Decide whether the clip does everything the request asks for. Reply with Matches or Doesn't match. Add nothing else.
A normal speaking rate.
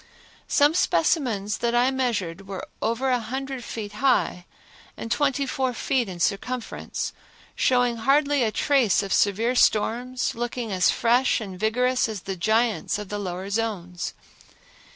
Matches